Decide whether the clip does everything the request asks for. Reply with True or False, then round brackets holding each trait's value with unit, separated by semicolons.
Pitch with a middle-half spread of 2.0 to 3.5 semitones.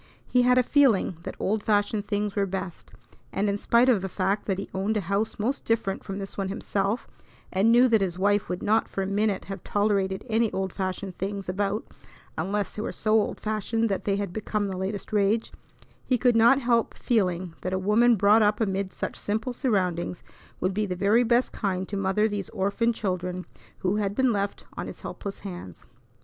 True (2.4 semitones)